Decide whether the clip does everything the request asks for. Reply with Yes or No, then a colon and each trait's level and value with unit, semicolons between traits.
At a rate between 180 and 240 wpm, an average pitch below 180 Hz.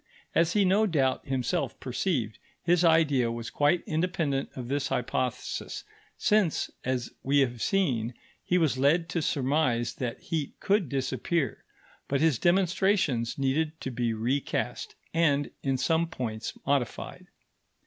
No: slow, 135 wpm; medium, 140 Hz